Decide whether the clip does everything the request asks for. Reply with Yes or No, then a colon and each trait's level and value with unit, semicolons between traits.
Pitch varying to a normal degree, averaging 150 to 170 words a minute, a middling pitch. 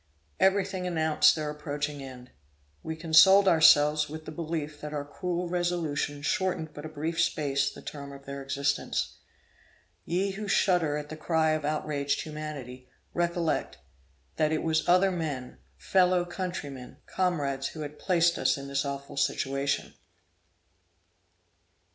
No: average, 3.4 semitones; average, 140 wpm; medium, 155 Hz